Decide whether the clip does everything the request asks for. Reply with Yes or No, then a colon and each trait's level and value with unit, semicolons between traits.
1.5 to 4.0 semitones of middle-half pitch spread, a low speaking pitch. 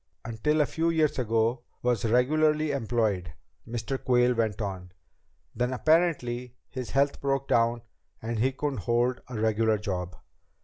Yes: average, 3.6 semitones; low, 120 Hz